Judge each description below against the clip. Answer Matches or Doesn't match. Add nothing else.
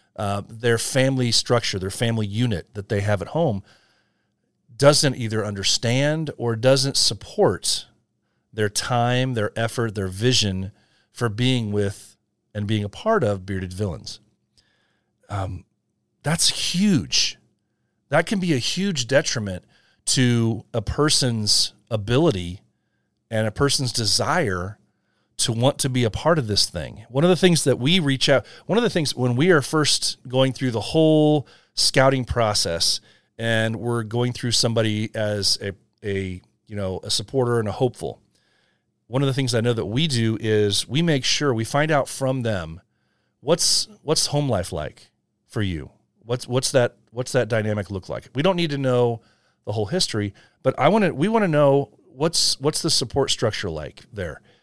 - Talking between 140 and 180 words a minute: Matches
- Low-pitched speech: Matches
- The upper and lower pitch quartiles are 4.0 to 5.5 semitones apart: Matches